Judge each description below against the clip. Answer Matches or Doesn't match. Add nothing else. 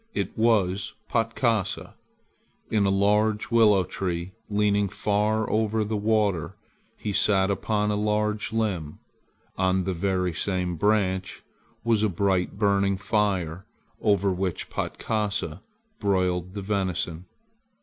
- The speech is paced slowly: Matches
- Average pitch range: Doesn't match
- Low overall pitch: Matches